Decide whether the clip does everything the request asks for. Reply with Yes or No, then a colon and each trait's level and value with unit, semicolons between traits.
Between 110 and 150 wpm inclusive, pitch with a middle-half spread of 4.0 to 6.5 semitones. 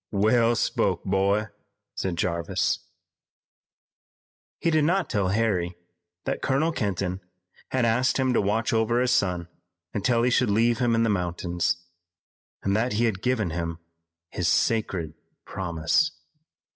Yes: slow, 135 wpm; average, 4.9 semitones